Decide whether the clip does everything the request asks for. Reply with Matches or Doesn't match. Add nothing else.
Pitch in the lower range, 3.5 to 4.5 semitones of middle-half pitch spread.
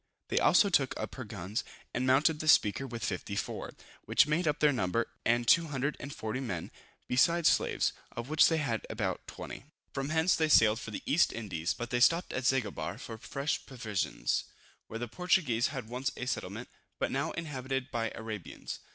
Doesn't match